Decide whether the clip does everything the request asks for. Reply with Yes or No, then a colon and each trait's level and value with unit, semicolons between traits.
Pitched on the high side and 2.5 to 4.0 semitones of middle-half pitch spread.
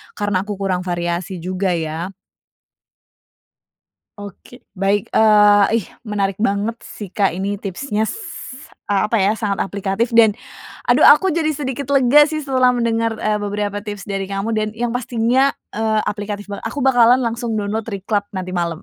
Yes: high, 210 Hz; average, 2.9 semitones